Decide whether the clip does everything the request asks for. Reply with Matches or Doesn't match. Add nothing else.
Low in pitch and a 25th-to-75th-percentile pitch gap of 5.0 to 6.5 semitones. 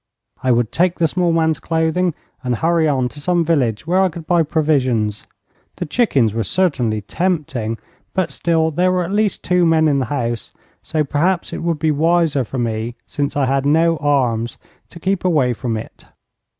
Doesn't match